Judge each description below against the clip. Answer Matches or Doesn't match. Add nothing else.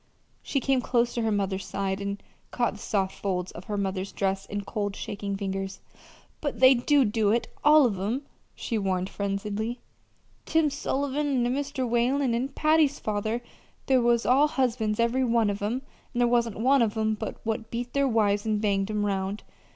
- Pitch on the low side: Doesn't match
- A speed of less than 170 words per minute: Doesn't match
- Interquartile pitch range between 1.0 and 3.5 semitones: Doesn't match